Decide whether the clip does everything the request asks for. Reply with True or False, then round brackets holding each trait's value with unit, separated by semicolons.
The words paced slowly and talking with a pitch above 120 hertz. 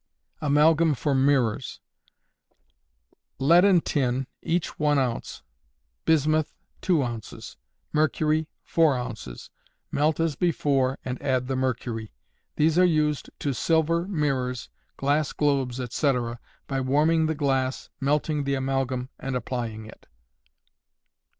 True (115 wpm; 140 Hz)